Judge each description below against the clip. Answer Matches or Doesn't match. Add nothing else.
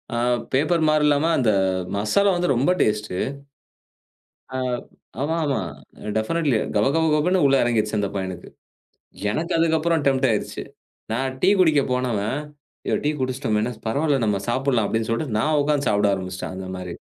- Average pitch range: Doesn't match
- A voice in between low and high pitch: Doesn't match